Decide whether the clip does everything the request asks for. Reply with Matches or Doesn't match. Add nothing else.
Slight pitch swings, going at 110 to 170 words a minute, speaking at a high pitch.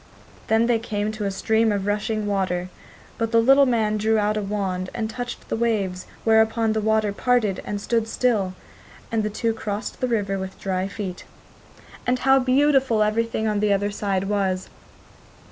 Doesn't match